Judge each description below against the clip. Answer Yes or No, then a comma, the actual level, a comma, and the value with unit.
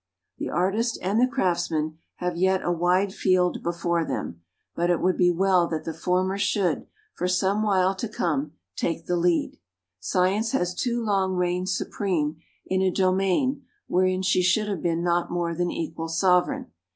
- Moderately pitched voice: Yes, medium, 180 Hz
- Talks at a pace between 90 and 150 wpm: No, average, 170 wpm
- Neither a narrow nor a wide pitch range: No, narrow, 1.9 semitones